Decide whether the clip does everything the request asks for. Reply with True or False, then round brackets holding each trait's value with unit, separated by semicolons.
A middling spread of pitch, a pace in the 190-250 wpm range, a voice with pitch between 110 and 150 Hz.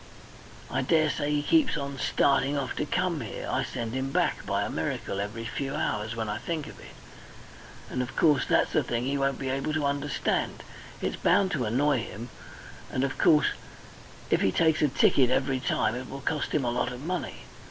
True (3.3 semitones; 205 wpm; 135 Hz)